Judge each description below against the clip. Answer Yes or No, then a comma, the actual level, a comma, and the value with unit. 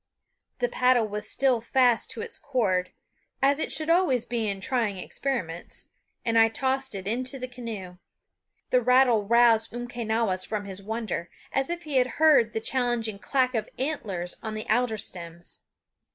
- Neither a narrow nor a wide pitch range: Yes, average, 3.6 semitones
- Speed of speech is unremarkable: Yes, average, 165 wpm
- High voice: Yes, high, 235 Hz